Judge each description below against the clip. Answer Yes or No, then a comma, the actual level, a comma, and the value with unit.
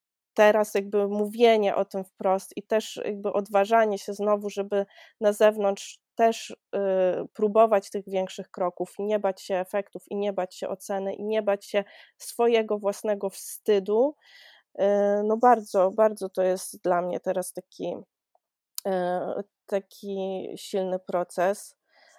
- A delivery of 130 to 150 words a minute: Yes, average, 140 wpm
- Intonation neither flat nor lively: No, narrow, 1.9 semitones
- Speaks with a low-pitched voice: No, high, 200 Hz